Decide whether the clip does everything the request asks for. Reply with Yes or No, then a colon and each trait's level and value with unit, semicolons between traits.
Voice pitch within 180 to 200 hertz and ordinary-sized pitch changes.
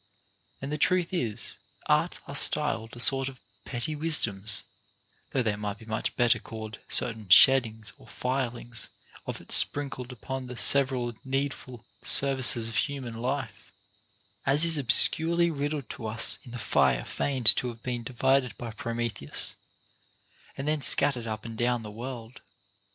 No: low, 125 Hz; average, 3.3 semitones